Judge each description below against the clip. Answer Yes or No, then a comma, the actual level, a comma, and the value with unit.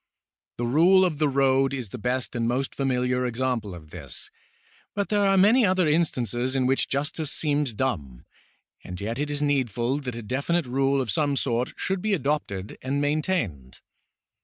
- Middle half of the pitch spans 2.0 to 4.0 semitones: Yes, average, 3.7 semitones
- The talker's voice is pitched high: No, low, 135 Hz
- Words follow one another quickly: No, average, 175 wpm